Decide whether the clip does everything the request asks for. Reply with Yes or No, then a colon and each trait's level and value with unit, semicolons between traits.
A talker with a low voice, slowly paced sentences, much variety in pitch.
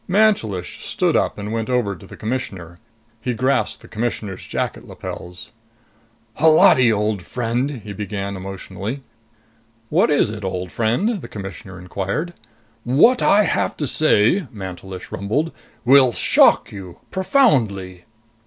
Yes: low, 110 Hz; slow, 130 wpm; wide, 6.1 semitones